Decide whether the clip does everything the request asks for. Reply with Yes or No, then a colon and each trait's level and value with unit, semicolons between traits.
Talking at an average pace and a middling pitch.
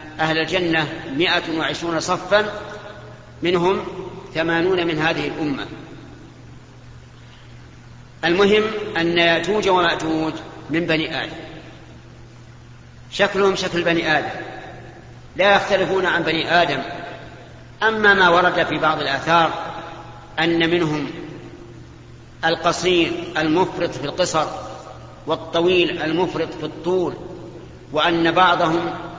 Yes: average, 90 wpm; medium, 165 Hz